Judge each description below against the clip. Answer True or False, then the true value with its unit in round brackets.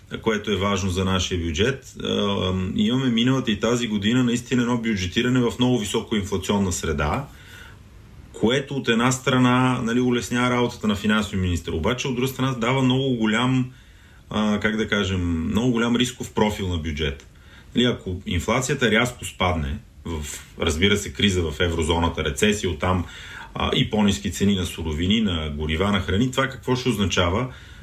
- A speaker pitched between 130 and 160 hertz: False (105 Hz)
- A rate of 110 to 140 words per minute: False (155 wpm)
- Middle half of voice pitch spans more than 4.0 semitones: True (5.1 semitones)